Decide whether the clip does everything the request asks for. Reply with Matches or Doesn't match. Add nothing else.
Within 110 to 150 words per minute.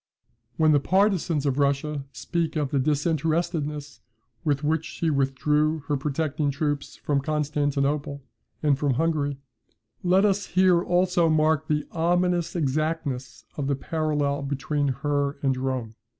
Matches